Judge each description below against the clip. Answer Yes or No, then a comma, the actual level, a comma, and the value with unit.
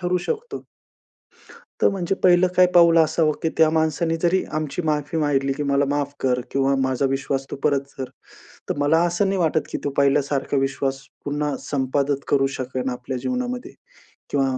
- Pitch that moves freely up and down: No, average, 3.6 semitones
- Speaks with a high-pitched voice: No, medium, 145 Hz